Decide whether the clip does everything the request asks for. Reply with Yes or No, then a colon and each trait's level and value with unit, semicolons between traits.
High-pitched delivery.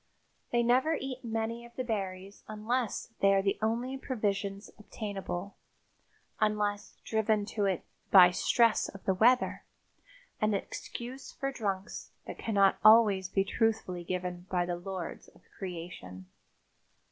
Yes: high, 205 Hz